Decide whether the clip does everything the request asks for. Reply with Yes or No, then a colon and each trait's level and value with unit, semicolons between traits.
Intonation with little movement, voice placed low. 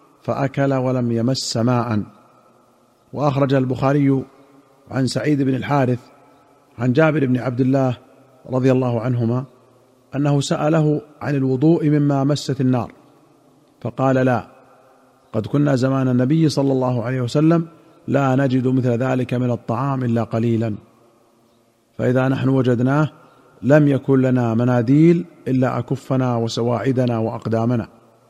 Yes: narrow, 2.3 semitones; low, 130 Hz